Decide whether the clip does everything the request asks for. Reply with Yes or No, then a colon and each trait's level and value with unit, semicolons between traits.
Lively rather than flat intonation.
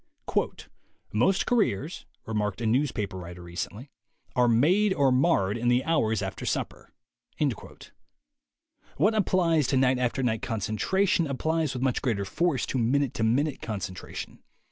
Yes: wide, 6.2 semitones